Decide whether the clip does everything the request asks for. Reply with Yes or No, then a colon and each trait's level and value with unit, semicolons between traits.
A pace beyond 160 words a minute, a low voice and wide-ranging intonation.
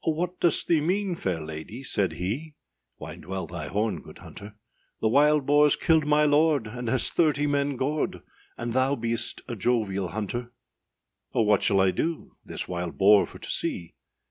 Yes: average, 180 wpm; low, 120 Hz; wide, 7.1 semitones